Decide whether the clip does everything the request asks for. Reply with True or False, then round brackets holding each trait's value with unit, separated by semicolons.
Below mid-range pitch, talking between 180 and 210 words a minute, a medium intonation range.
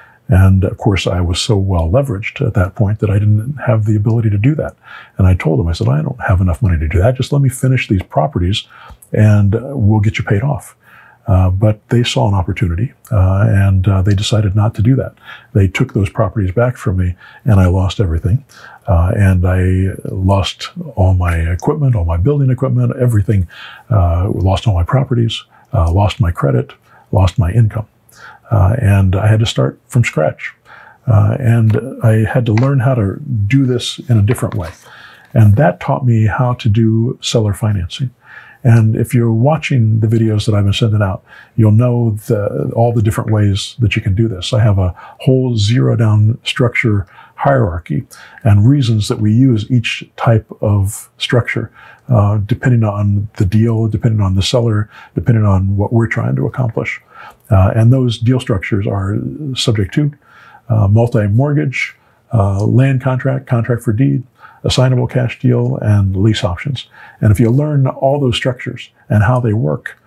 True (110 Hz; 185 wpm; 3.4 semitones)